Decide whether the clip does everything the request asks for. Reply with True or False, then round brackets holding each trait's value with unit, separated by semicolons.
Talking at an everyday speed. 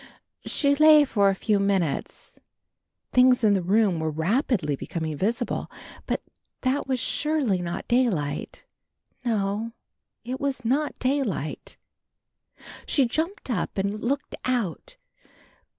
False (120 wpm)